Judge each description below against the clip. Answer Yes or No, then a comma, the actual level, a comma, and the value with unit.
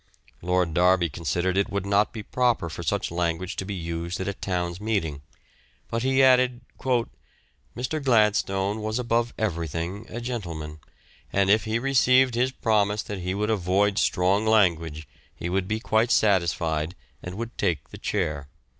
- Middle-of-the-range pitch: No, low, 100 Hz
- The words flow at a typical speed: Yes, average, 160 wpm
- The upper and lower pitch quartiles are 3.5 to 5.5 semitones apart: Yes, average, 4.2 semitones